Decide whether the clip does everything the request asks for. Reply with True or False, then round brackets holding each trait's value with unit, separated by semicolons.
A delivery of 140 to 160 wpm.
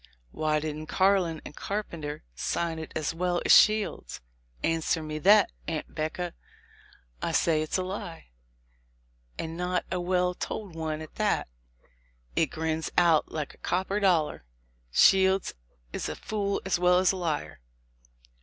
True (145 wpm)